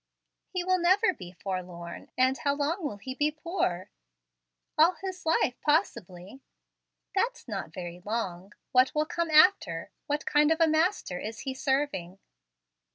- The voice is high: Yes, very high, 280 Hz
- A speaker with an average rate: Yes, average, 150 wpm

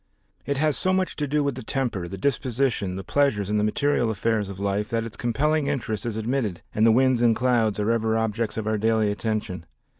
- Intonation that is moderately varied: Yes, average, 4.1 semitones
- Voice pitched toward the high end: No, low, 115 Hz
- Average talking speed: No, fast, 220 wpm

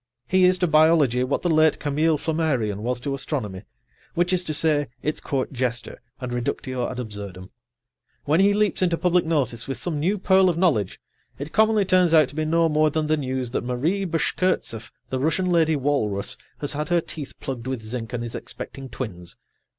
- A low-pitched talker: No, medium, 150 Hz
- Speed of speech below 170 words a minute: No, average, 195 wpm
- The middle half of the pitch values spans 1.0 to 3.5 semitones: No, average, 5.0 semitones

